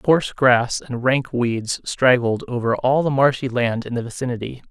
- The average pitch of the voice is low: Yes, low, 125 Hz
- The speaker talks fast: No, average, 180 wpm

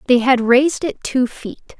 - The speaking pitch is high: Yes, very high, 255 Hz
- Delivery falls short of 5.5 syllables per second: Yes, 4.5 syllables/s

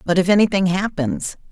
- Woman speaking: Yes, female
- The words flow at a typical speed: Yes, average, 160 wpm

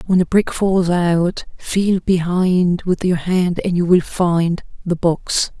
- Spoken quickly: No, average, 170 wpm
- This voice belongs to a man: No, female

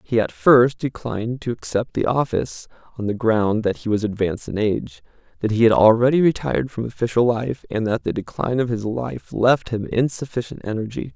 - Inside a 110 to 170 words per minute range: No, average, 195 wpm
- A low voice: Yes, low, 110 Hz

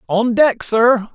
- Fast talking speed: No, average, 155 wpm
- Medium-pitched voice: No, high, 230 Hz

